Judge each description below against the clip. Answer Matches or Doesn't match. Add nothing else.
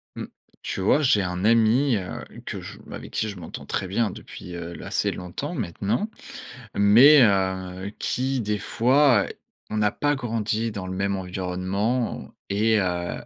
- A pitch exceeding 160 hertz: Doesn't match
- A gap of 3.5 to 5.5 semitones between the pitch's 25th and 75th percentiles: Matches